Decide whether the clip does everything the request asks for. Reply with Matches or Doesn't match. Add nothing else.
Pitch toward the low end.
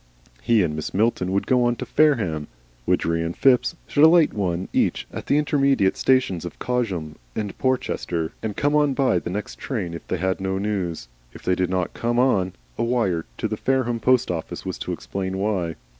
Matches